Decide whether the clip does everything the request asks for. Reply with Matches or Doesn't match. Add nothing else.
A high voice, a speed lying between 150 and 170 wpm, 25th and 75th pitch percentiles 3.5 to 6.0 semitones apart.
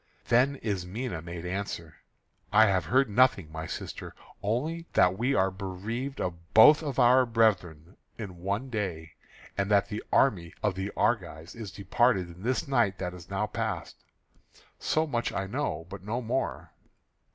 Doesn't match